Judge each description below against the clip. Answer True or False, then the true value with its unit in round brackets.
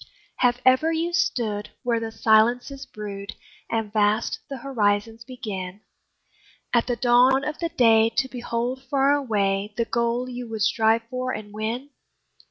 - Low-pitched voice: False (235 Hz)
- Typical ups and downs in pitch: True (3.0 semitones)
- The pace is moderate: True (150 wpm)